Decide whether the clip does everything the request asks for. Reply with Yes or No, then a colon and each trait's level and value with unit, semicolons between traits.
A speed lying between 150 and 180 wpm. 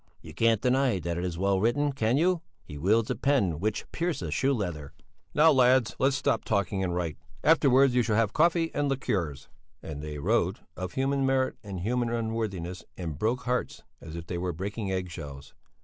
No: average, 190 wpm